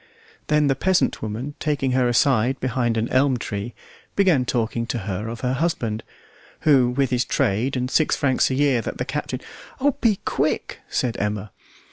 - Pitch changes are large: No, average, 3.4 semitones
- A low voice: Yes, low, 125 Hz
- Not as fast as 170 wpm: No, average, 175 wpm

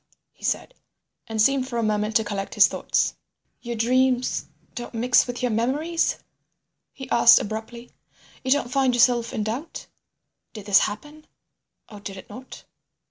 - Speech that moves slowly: No, average, 155 wpm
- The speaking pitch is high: Yes, high, 240 Hz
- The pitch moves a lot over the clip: No, average, 3.1 semitones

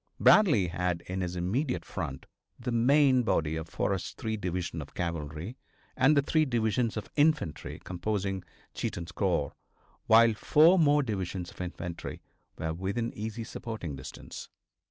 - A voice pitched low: Yes, low, 100 Hz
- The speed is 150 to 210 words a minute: No, average, 140 wpm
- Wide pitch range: Yes, wide, 6.2 semitones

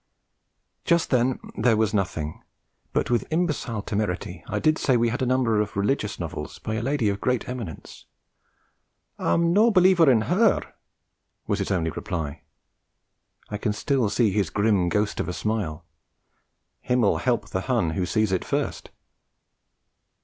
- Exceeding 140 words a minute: Yes, average, 155 wpm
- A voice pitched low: Yes, low, 110 Hz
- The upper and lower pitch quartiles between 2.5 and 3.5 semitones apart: No, average, 4.6 semitones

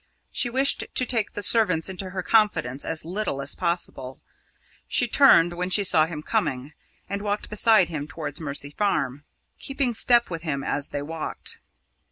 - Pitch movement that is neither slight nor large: No, wide, 6.2 semitones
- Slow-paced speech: No, average, 170 wpm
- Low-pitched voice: No, medium, 175 Hz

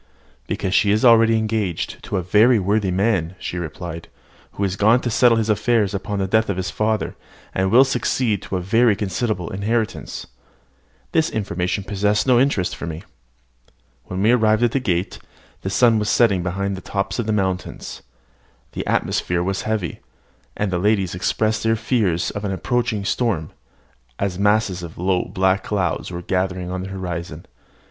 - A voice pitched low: Yes, low, 100 Hz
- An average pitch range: Yes, average, 3.2 semitones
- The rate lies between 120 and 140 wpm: No, average, 175 wpm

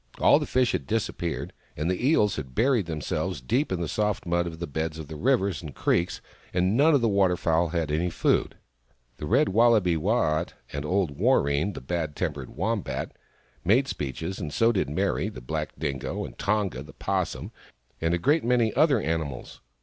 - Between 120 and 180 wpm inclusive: No, average, 190 wpm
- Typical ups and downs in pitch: No, wide, 5.7 semitones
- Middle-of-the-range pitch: No, very low, 85 Hz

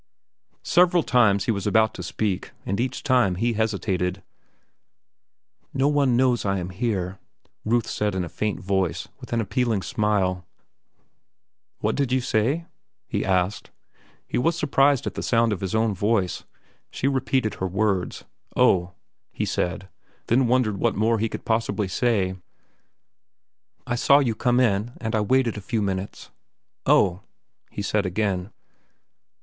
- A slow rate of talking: No, average, 145 wpm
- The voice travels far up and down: No, average, 4.1 semitones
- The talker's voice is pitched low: Yes, low, 110 Hz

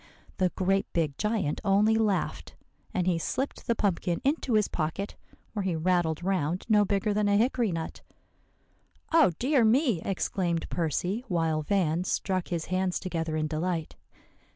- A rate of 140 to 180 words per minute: Yes, average, 155 wpm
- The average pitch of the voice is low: No, medium, 185 Hz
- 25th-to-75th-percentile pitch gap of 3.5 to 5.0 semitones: Yes, average, 4.0 semitones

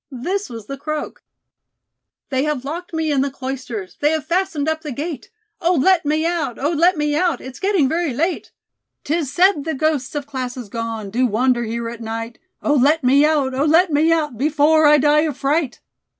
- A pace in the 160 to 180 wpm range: No, average, 200 wpm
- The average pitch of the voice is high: Yes, very high, 290 Hz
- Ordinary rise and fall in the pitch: Yes, average, 3.7 semitones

